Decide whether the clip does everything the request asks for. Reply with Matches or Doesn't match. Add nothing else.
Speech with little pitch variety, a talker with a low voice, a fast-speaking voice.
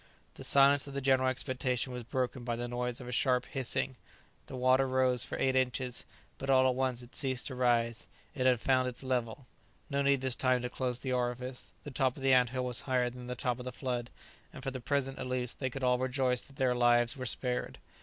Matches